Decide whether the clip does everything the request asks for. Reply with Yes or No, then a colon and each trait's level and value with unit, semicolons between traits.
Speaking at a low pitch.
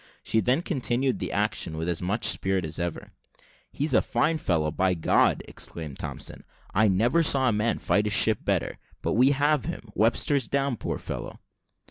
Yes: low, 110 Hz